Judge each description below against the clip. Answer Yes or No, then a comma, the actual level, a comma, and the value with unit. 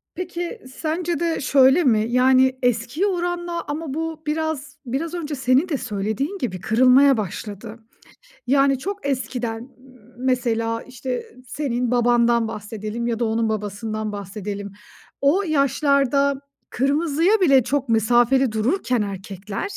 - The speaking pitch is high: Yes, very high, 255 Hz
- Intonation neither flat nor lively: Yes, average, 5.0 semitones